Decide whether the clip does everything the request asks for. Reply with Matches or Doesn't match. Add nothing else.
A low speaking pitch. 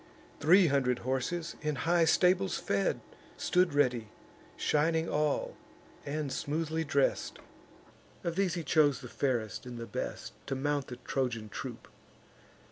Doesn't match